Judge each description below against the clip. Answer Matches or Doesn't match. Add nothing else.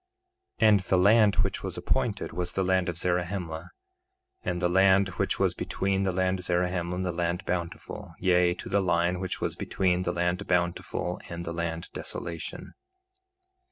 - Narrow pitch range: Matches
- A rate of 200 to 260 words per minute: Doesn't match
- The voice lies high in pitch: Doesn't match